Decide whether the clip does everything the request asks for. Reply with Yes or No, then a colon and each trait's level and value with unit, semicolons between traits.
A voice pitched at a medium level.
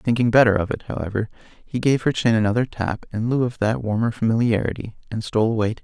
No: low, 115 Hz